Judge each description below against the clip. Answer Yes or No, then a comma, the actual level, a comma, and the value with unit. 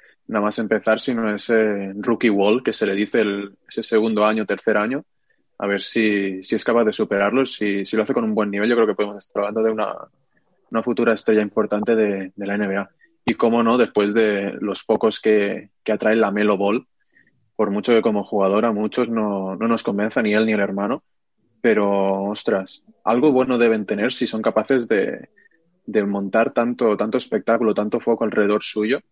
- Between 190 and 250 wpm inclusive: Yes, average, 200 wpm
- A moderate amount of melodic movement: No, narrow, 2.0 semitones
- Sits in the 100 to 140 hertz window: Yes, low, 105 Hz